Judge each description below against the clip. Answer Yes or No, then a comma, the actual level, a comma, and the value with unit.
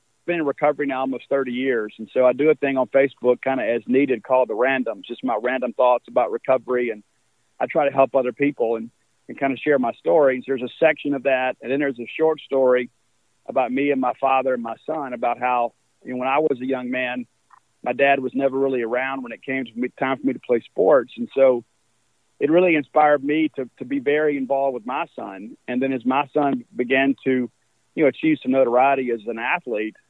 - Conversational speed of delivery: No, fast, 235 wpm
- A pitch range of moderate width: No, narrow, 2.1 semitones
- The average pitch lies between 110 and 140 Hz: Yes, low, 130 Hz